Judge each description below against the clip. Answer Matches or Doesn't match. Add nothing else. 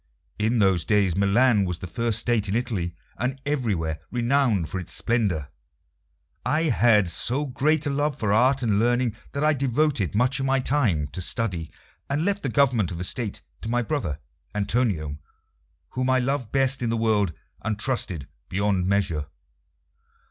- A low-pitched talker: Matches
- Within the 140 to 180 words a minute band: Matches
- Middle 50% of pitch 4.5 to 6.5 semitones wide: Matches